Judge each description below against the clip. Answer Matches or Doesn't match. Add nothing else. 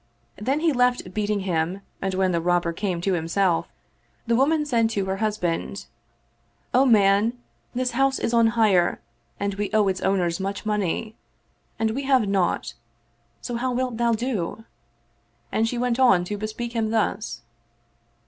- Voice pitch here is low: Doesn't match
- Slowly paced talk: Doesn't match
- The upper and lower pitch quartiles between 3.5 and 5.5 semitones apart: Matches